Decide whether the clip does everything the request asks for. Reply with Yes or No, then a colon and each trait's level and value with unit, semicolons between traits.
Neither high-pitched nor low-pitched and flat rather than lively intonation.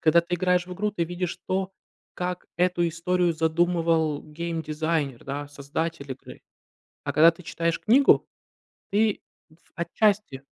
Yes: medium, 170 Hz; narrow, 2.3 semitones